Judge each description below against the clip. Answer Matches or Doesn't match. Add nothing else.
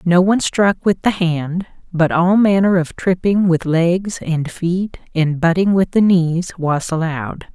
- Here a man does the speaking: Doesn't match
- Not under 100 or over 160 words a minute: Doesn't match